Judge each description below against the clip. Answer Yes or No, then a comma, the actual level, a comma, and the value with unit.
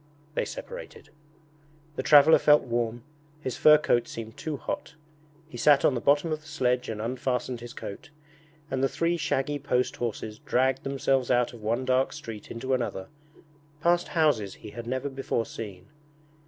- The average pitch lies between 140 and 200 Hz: No, low, 130 Hz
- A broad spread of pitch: No, average, 3.9 semitones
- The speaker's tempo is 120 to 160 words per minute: No, average, 170 wpm